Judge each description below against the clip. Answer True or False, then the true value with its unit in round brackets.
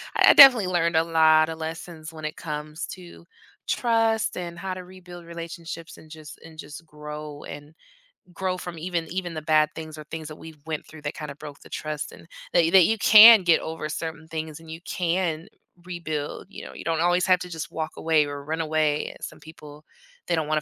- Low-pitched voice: False (160 Hz)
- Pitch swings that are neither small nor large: False (2.3 semitones)